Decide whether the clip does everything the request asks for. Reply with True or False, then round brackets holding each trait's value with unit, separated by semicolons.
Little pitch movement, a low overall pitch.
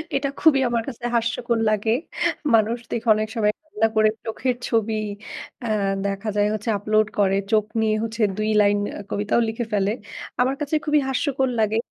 False (2.1 semitones; 220 Hz)